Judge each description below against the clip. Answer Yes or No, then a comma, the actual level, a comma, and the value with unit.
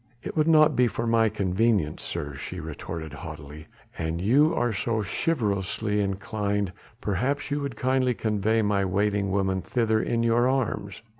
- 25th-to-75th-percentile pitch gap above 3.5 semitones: Yes, average, 3.9 semitones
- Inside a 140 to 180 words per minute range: Yes, average, 155 wpm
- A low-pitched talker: Yes, low, 105 Hz